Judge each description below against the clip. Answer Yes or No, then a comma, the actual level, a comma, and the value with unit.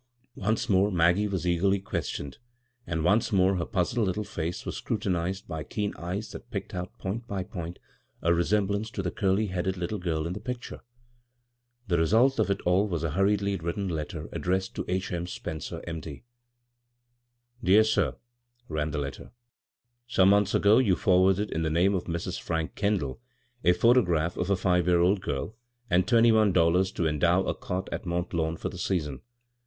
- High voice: No, very low, 95 Hz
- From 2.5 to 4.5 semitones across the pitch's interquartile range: Yes, average, 3.3 semitones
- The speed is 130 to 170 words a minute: No, average, 200 wpm